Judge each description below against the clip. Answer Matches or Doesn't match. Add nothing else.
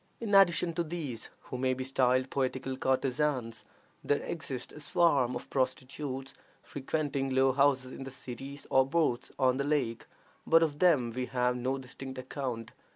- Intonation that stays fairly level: Matches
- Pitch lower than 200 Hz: Matches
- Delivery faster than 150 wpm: Matches